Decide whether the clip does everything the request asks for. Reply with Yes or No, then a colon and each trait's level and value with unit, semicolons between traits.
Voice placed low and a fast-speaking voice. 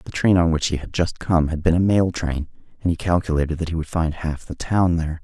Yes: very low, 85 Hz; fast, 275 wpm